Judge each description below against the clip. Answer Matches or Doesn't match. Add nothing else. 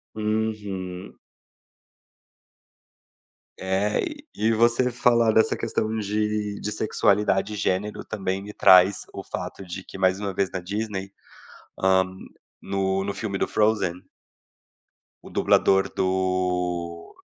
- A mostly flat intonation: Matches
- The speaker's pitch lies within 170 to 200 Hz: Doesn't match